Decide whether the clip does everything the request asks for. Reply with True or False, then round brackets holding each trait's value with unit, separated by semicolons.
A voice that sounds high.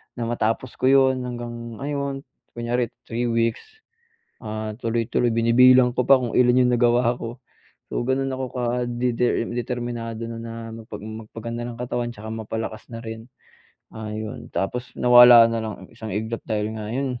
False (120 Hz)